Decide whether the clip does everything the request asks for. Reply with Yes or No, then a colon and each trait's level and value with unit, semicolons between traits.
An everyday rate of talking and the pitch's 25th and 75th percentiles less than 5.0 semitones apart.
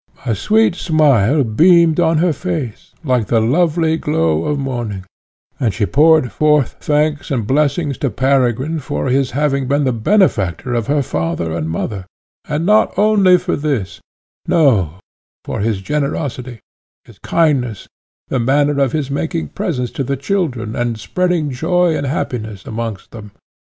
No: average, 150 wpm; wide, 5.5 semitones